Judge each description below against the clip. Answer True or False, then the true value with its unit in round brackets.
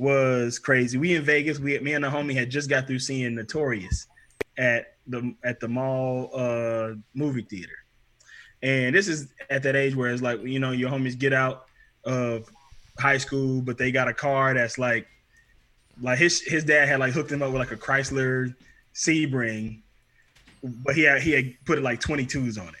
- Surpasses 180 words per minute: True (195 wpm)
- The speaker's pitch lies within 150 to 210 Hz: False (130 Hz)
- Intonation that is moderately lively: False (2.2 semitones)